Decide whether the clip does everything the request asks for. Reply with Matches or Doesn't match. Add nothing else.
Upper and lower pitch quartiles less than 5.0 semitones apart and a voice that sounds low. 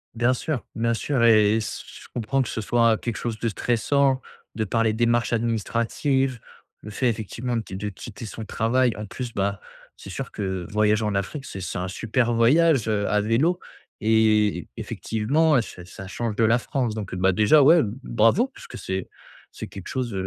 Matches